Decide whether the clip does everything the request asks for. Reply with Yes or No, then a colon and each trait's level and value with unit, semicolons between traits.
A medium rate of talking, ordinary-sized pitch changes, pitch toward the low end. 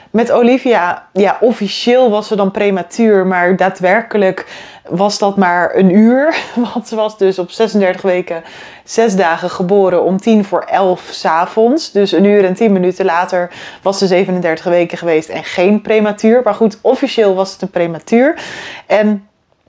No: average, 160 wpm; average, 3.4 semitones; high, 200 Hz